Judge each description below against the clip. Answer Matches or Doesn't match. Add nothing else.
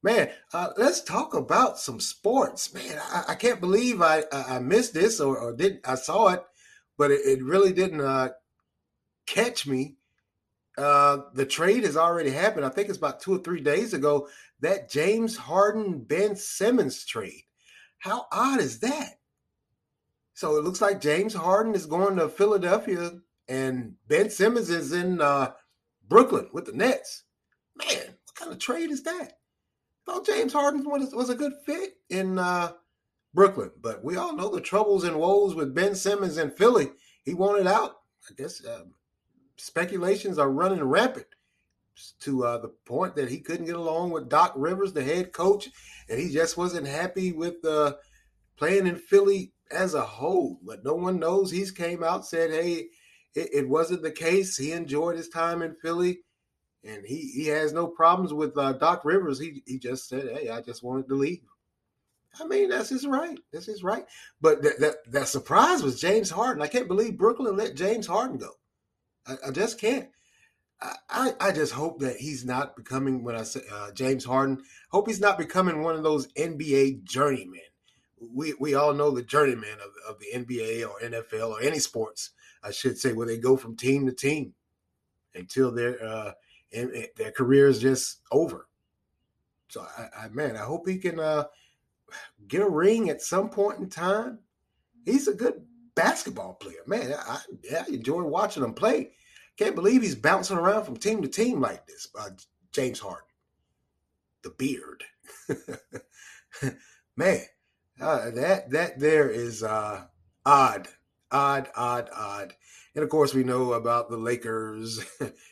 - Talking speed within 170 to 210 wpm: Matches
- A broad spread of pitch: Matches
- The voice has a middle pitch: Matches